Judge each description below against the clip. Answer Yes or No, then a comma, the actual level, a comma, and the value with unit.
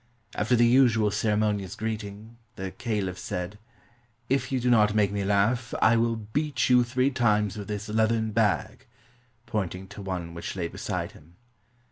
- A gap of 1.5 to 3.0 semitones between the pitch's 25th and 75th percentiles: Yes, narrow, 2.6 semitones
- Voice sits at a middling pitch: No, low, 105 Hz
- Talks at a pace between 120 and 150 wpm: No, average, 160 wpm